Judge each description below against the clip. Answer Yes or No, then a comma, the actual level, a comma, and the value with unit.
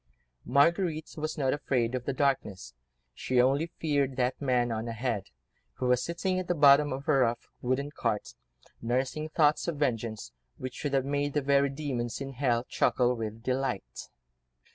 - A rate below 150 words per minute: No, average, 165 wpm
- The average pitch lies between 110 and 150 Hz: Yes, low, 135 Hz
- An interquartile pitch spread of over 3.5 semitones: No, average, 3.1 semitones